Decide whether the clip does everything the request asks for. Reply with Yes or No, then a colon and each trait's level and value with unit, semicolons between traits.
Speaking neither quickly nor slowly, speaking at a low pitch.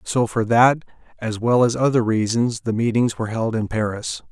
Yes: average, 195 wpm; low, 115 Hz